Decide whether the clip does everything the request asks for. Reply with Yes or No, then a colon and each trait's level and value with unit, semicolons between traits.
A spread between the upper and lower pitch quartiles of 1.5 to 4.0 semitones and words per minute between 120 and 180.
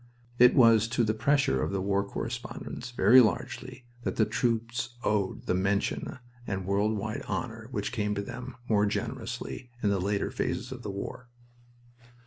Yes: average, 3.3 semitones; average, 165 wpm